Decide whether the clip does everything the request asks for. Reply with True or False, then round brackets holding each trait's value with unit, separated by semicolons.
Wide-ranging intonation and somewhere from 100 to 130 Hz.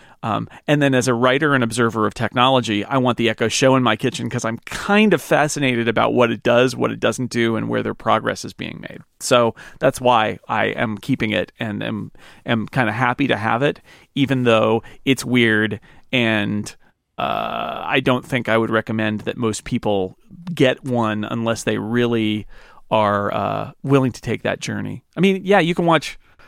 False (3.2 semitones; 120 Hz)